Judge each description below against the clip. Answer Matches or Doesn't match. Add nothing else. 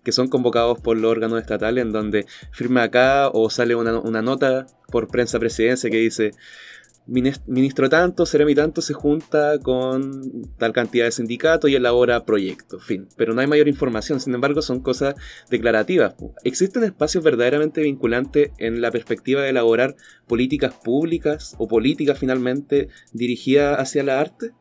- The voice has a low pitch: Matches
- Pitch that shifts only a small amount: Doesn't match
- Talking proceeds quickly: Doesn't match